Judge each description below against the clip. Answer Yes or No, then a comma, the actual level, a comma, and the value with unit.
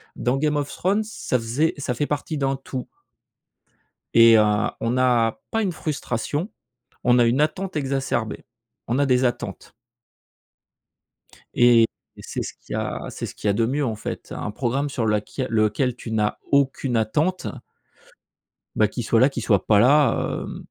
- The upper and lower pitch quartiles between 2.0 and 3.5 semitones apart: No, average, 4.0 semitones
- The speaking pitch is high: No, low, 125 Hz